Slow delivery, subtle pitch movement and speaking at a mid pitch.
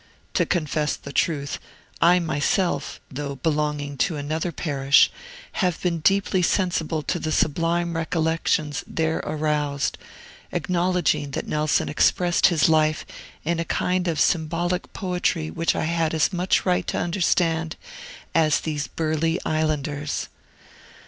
Yes: slow, 130 wpm; narrow, 2.3 semitones; medium, 160 Hz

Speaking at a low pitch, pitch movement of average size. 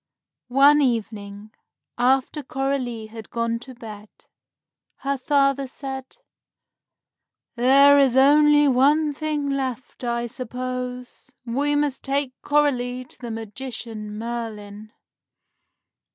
No: very high, 255 Hz; average, 3.1 semitones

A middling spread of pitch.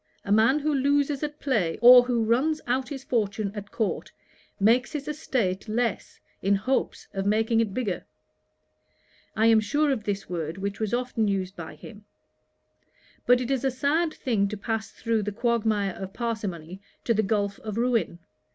Yes: average, 4.0 semitones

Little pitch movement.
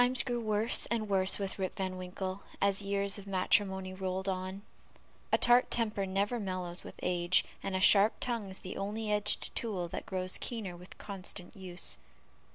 Yes: narrow, 2.0 semitones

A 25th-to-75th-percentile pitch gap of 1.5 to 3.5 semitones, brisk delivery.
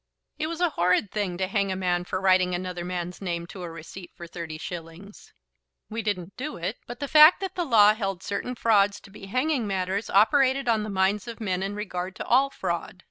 No: average, 4.1 semitones; fast, 220 wpm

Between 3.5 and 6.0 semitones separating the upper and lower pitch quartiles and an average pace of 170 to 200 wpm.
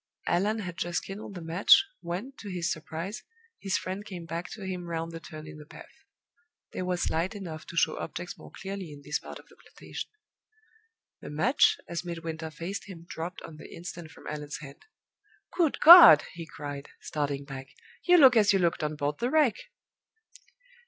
Yes: average, 3.8 semitones; average, 185 wpm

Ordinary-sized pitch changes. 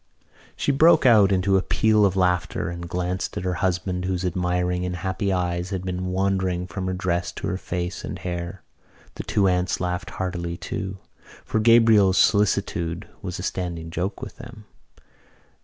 No: narrow, 1.6 semitones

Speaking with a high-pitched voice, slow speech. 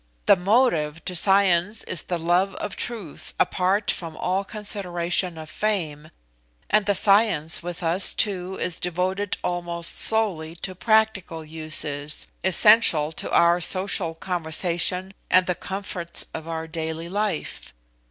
No: medium, 180 Hz; slow, 130 wpm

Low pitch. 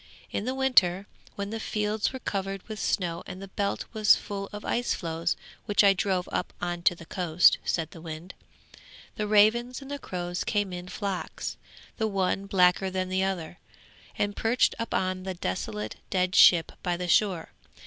No: high, 190 Hz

